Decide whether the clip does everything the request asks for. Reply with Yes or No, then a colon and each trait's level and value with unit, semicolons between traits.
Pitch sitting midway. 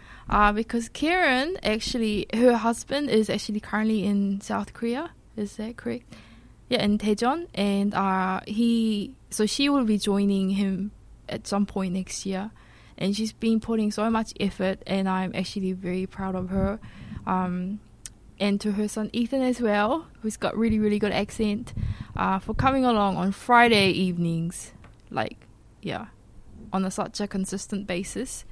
No: high, 205 Hz